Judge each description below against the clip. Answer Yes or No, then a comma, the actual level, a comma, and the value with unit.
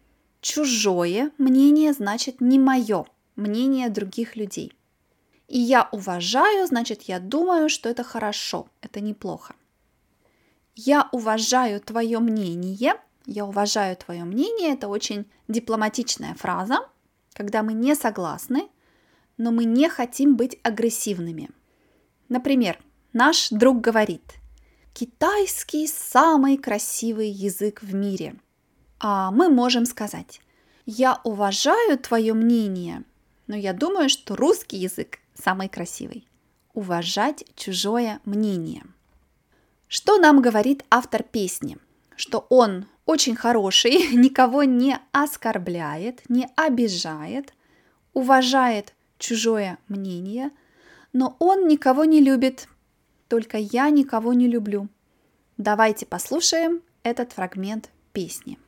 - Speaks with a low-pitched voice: No, high, 235 Hz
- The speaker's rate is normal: No, slow, 105 wpm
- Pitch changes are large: No, average, 4.5 semitones